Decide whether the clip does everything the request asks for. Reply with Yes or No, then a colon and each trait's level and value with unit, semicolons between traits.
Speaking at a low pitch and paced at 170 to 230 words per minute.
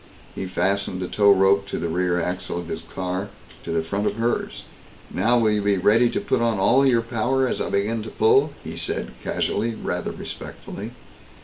Yes: low, 100 Hz; average, 200 wpm